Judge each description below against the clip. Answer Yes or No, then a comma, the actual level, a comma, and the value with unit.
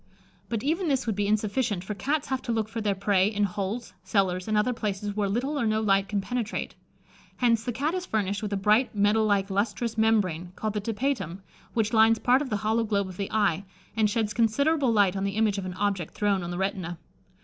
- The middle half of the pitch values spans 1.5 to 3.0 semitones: Yes, narrow, 2.6 semitones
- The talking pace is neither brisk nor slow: No, fast, 225 wpm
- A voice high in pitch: Yes, high, 210 Hz